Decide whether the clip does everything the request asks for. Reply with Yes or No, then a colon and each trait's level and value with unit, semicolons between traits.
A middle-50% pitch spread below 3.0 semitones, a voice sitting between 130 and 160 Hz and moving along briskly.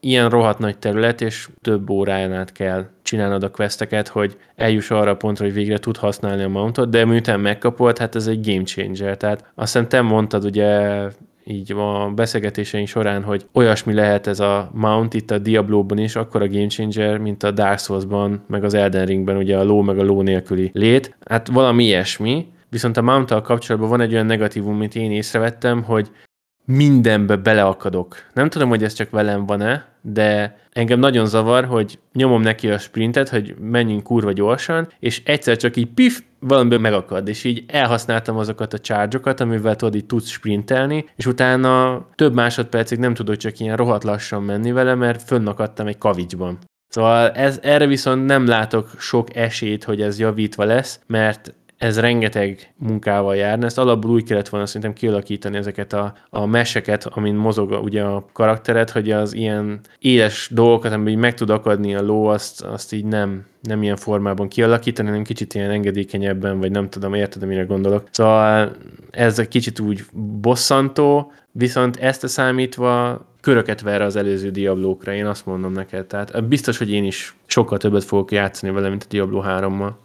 No: narrow, 2.5 semitones; low, 110 Hz; fast, 180 wpm